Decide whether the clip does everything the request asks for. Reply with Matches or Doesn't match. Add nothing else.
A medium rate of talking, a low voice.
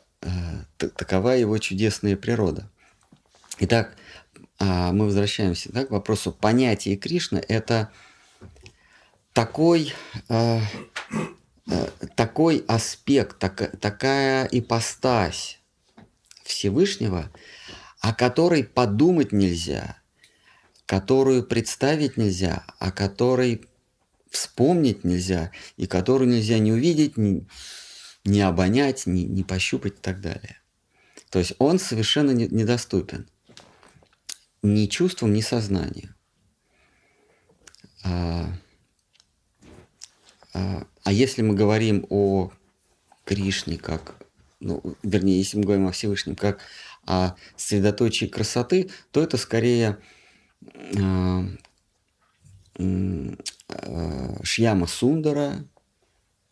Doesn't match